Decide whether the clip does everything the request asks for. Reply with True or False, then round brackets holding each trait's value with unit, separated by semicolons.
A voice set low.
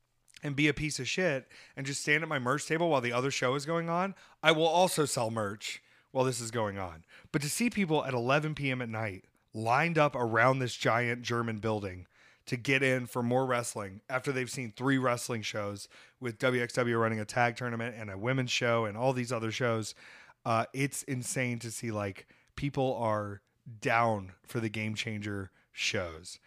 True (125 Hz)